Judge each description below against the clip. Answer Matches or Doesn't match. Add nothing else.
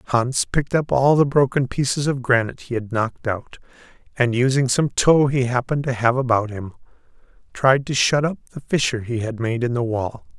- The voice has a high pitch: Doesn't match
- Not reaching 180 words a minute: Doesn't match